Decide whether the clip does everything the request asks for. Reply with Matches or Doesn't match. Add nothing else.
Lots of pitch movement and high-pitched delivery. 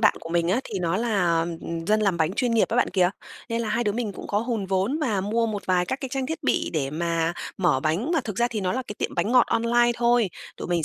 Doesn't match